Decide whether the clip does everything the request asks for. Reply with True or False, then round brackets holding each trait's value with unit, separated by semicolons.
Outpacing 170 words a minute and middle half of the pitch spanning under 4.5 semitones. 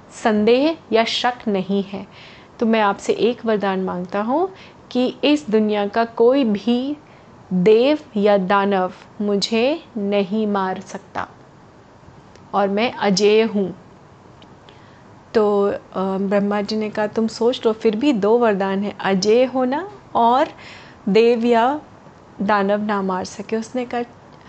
False (130 wpm; 2.9 semitones)